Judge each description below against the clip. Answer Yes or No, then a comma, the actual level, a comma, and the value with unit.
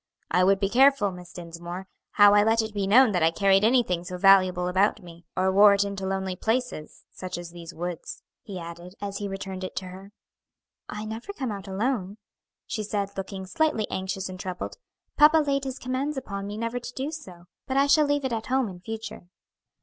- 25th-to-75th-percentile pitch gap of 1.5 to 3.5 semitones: No, average, 3.9 semitones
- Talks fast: Yes, fast, 210 wpm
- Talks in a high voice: Yes, high, 200 Hz